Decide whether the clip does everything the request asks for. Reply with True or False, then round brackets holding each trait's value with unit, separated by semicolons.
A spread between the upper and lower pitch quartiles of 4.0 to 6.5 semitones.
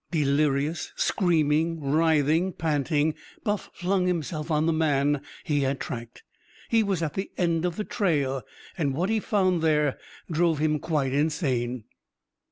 False (3.2 semitones)